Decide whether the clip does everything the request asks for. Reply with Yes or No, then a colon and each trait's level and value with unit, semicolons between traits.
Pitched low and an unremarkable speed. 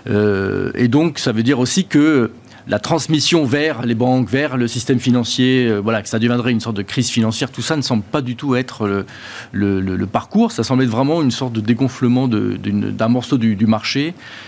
Yes: low, 125 Hz; average, 210 wpm